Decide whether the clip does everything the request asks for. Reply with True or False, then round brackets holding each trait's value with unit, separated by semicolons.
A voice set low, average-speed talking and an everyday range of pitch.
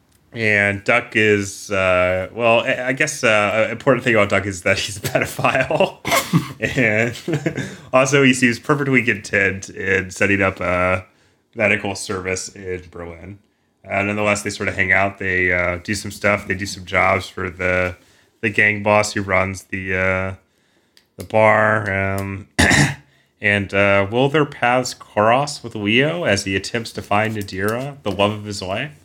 True (100 Hz; 165 wpm; 3.3 semitones)